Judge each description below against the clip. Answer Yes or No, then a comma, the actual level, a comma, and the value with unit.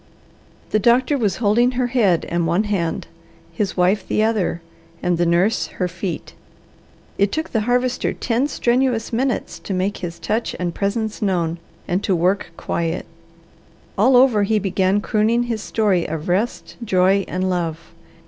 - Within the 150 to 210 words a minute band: Yes, average, 160 wpm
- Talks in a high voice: Yes, high, 200 Hz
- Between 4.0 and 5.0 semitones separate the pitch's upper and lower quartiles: Yes, average, 4.4 semitones